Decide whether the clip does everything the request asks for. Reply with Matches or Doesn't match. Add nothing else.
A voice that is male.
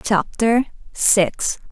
Doesn't match